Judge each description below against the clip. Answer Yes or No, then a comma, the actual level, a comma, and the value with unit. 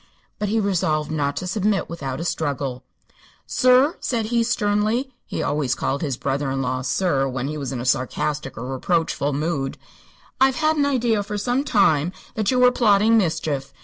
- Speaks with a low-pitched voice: No, medium, 170 Hz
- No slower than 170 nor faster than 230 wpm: Yes, average, 180 wpm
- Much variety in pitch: Yes, wide, 8.3 semitones